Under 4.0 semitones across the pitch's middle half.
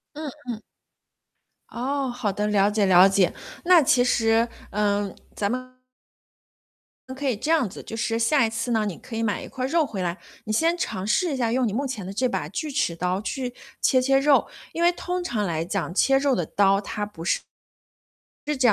No: average, 4.9 semitones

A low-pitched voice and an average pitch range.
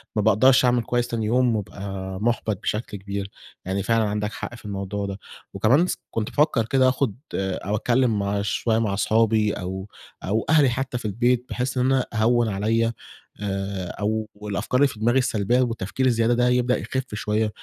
Yes: low, 110 Hz; average, 3.3 semitones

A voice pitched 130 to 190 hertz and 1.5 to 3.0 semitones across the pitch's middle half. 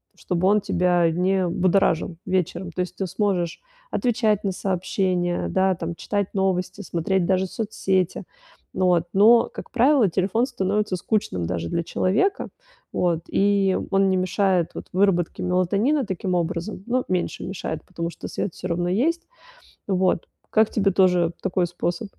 Yes: medium, 185 Hz; narrow, 2.4 semitones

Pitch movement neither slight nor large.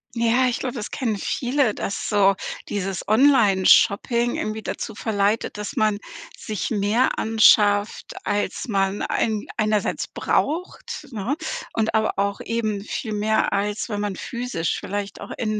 No: narrow, 2.3 semitones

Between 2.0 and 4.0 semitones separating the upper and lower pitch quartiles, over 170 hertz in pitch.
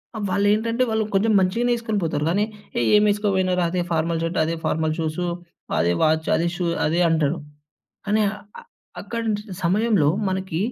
No: average, 4.6 semitones; medium, 185 Hz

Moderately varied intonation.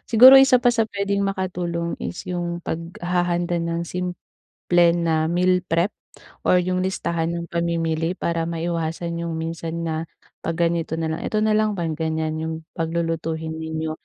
No: narrow, 1.8 semitones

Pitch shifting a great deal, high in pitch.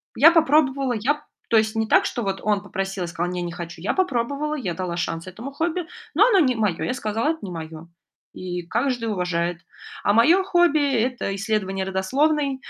Yes: wide, 7.5 semitones; high, 220 Hz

